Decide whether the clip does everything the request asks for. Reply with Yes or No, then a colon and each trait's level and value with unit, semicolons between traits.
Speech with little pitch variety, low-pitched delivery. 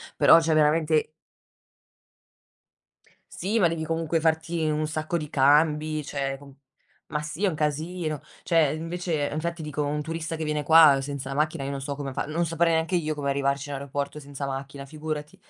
No: narrow, 2.3 semitones; medium, 155 Hz